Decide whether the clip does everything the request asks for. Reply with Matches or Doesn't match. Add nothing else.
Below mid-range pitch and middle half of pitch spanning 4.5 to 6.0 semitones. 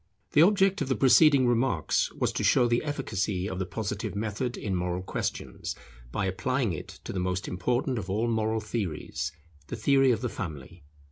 Matches